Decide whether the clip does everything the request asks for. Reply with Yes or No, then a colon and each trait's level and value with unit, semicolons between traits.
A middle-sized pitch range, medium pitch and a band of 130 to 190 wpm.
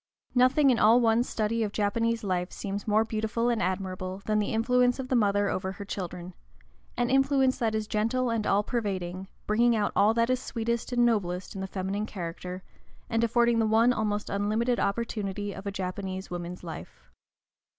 No: average, 3.3 semitones; high, 215 Hz; average, 180 wpm